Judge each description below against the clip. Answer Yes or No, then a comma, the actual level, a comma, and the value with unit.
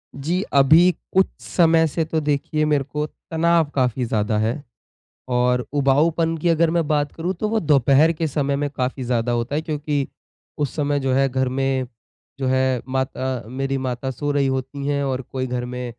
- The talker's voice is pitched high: No, medium, 140 Hz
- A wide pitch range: No, average, 3.0 semitones